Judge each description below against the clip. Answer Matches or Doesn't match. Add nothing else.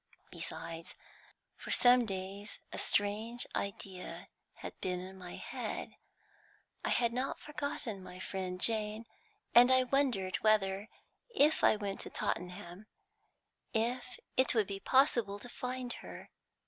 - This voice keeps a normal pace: Doesn't match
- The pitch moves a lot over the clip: Doesn't match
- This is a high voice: Matches